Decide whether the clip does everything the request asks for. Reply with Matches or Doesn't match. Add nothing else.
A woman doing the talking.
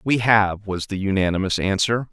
Doesn't match